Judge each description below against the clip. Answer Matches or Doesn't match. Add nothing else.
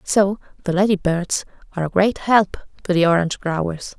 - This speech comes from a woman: Matches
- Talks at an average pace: Matches